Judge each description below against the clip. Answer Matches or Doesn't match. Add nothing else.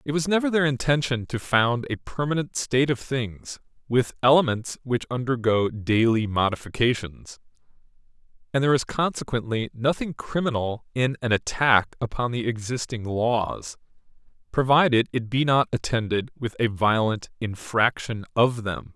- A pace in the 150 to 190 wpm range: Doesn't match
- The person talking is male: Matches